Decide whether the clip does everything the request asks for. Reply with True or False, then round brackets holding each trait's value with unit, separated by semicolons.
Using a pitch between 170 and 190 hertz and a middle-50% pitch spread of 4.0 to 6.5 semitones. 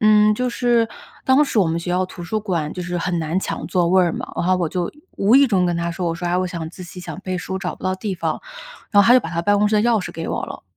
False (185 Hz; 3.3 semitones)